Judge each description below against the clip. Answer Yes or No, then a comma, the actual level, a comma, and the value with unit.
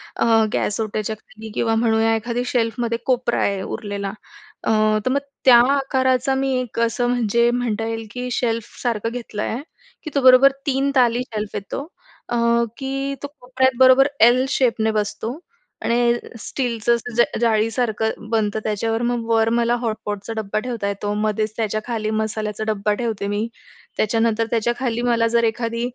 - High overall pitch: Yes, high, 230 Hz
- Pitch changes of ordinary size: No, narrow, 2.2 semitones